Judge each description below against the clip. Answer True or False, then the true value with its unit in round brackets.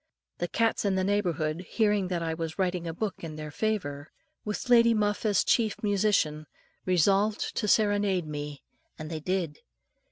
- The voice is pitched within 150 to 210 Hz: True (185 Hz)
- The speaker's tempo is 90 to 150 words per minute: False (165 wpm)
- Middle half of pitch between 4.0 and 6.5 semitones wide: True (4.6 semitones)